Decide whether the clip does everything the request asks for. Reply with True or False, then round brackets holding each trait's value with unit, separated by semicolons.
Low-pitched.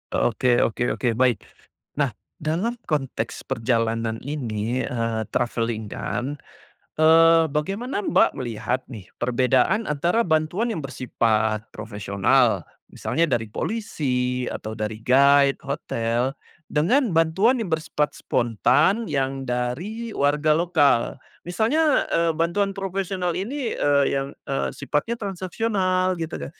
False (145 Hz)